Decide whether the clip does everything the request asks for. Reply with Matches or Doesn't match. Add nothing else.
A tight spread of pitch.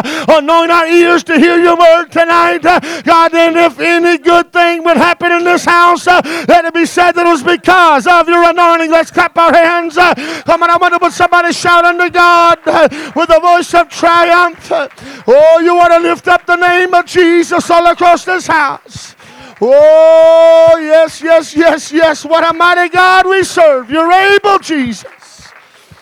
Matches